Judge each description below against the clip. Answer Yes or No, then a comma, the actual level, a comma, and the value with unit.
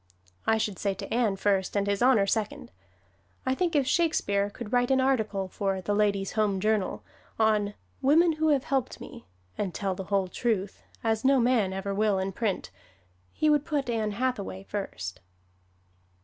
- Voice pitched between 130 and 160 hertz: No, high, 210 Hz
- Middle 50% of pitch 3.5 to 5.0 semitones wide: Yes, average, 4.5 semitones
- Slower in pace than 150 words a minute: No, average, 175 wpm